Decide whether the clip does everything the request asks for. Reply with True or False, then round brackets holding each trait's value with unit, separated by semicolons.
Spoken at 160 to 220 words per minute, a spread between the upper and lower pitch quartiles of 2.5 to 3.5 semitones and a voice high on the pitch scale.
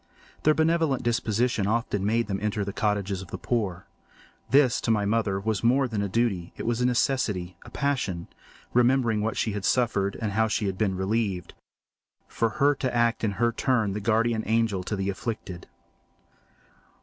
False (175 wpm; 3.1 semitones; 110 Hz)